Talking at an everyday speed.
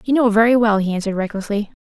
No: fast, 230 wpm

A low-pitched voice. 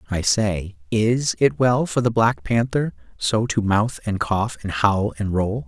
Yes: low, 110 Hz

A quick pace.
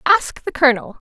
No: average, 165 wpm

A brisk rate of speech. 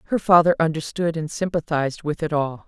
No: average, 180 wpm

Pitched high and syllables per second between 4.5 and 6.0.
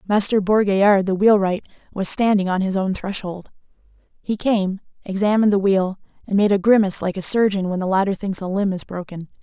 Yes: high, 195 Hz; 5.7 syllables/s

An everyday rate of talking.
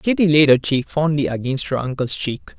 No: fast, 210 wpm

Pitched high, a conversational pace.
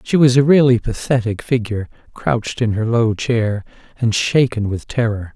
No: low, 115 Hz; average, 170 wpm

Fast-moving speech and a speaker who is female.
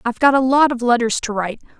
Yes: fast, 270 wpm; female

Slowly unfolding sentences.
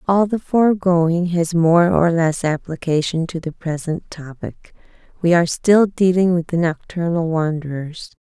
No: average, 145 wpm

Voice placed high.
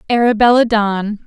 Yes: high, 220 Hz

